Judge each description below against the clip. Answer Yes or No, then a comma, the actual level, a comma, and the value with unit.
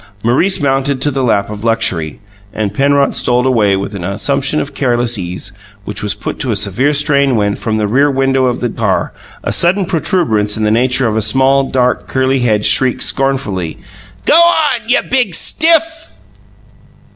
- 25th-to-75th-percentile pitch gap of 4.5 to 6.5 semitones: Yes, average, 4.8 semitones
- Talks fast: No, average, 180 wpm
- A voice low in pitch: Yes, low, 130 Hz